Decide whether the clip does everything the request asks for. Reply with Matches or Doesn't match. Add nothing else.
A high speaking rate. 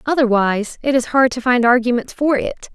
Doesn't match